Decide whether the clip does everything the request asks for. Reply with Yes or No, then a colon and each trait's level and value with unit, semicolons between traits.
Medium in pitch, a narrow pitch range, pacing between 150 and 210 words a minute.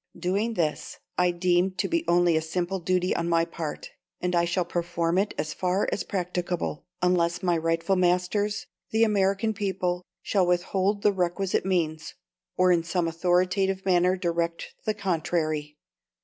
Yes: medium, 180 Hz; narrow, 2.1 semitones; average, 155 wpm